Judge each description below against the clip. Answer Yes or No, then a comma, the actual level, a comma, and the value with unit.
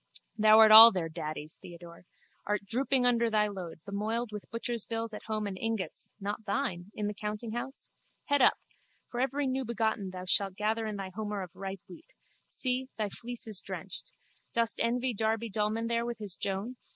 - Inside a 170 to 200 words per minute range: Yes, average, 175 wpm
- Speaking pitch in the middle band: No, high, 215 Hz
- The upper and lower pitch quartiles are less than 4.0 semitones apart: Yes, average, 2.9 semitones